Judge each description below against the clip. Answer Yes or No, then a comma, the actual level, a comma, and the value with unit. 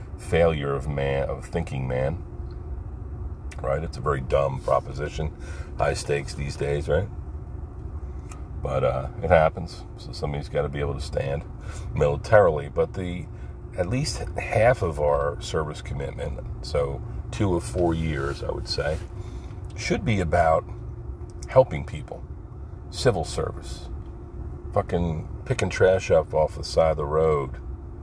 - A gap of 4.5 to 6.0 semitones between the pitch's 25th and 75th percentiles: No, average, 3.8 semitones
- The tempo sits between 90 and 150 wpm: Yes, slow, 135 wpm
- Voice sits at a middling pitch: No, very low, 80 Hz